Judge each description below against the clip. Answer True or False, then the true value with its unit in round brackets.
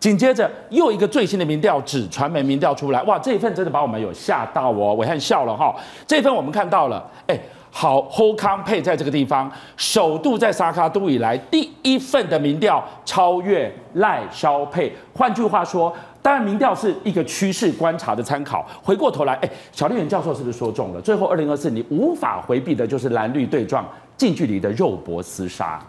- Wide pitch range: True (7.1 semitones)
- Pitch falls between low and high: True (180 Hz)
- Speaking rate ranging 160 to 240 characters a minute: False (315 characters per minute)